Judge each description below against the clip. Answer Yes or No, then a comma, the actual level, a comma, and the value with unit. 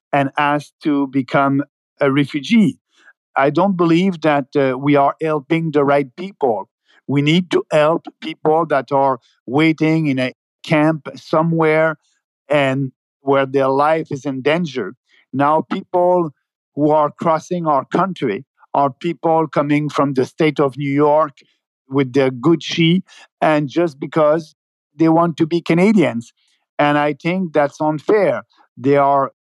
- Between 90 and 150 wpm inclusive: Yes, average, 140 wpm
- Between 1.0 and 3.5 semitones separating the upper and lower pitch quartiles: Yes, narrow, 2.6 semitones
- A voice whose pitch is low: No, medium, 150 Hz